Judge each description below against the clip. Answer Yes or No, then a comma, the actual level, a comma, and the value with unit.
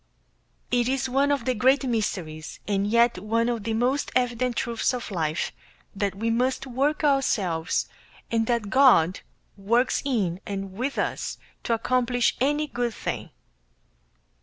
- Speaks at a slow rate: No, average, 145 wpm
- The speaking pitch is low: No, high, 235 Hz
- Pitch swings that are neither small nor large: Yes, average, 4.0 semitones